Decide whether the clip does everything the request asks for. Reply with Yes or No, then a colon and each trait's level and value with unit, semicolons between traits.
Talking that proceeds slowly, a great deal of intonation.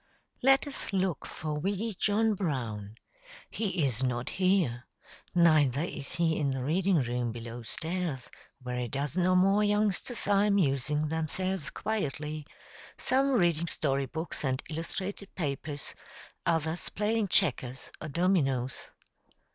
Yes: slow, 130 wpm; wide, 6.1 semitones